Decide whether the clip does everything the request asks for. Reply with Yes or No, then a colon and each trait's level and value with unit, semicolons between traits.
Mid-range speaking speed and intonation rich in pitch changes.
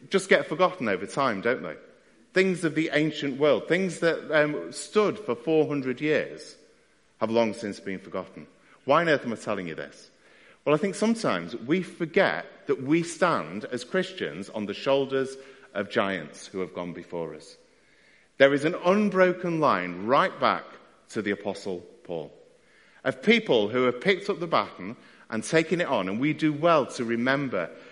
Yes: average, 175 wpm; wide, 6.6 semitones